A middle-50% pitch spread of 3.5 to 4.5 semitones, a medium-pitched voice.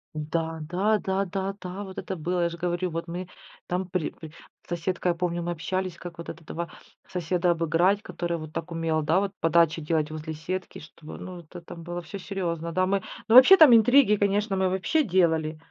No: narrow, 2.4 semitones; medium, 175 Hz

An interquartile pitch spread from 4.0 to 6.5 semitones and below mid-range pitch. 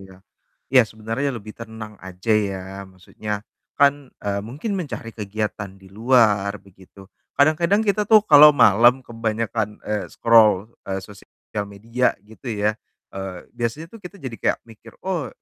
Yes: average, 4.3 semitones; low, 110 Hz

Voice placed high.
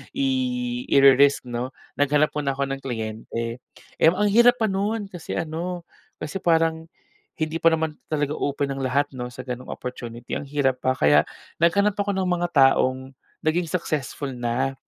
No: medium, 145 Hz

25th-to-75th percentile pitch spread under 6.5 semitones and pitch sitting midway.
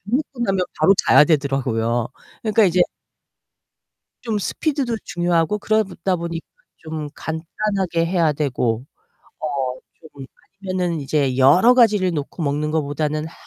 Yes: average, 5.1 semitones; medium, 165 Hz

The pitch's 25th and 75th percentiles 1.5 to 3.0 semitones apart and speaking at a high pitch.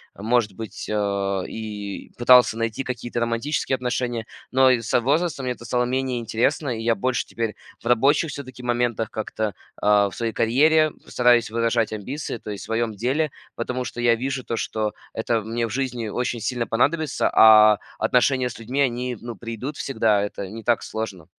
No: narrow, 2.4 semitones; low, 120 Hz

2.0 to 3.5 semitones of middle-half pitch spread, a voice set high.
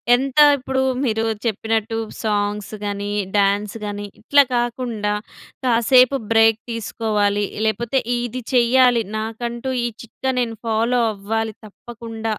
Yes: narrow, 2.4 semitones; high, 225 Hz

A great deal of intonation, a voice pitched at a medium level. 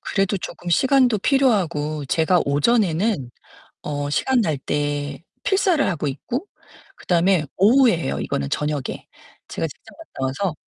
Yes: wide, 8.2 semitones; medium, 170 Hz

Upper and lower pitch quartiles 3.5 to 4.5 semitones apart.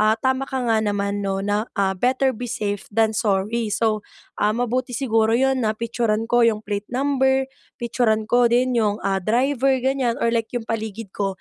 No: average, 2.8 semitones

